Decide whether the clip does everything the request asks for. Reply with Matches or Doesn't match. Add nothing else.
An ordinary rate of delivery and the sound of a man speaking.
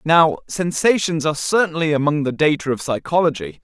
Matches